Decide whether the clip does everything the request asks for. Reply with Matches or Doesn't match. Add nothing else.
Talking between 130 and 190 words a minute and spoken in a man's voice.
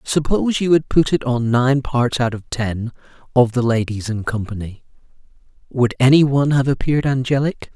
Matches